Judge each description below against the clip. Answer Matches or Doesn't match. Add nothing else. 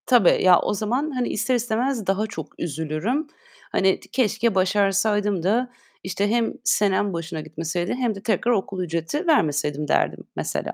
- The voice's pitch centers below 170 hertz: Doesn't match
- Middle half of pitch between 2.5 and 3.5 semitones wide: Doesn't match